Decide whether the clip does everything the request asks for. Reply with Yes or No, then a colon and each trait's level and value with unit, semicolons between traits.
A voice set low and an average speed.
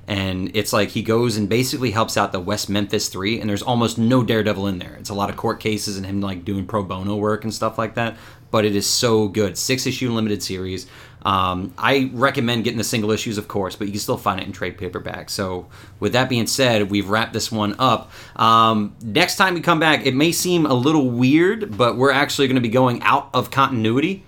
No: low, 110 Hz; fast, 235 wpm